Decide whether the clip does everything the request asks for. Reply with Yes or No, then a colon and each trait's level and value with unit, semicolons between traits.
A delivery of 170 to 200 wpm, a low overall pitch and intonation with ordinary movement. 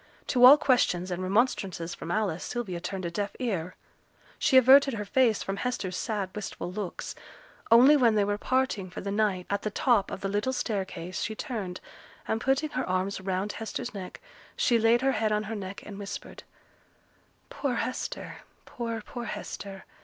No: average, 175 wpm; high, 210 Hz; average, 4.2 semitones